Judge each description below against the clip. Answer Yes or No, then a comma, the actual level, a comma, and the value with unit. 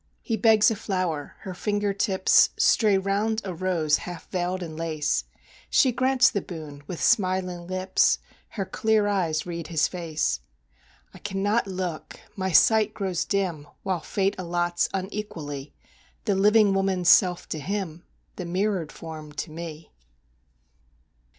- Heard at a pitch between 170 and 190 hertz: Yes, medium, 185 Hz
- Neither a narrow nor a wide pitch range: Yes, average, 3.4 semitones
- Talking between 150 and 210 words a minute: No, average, 140 wpm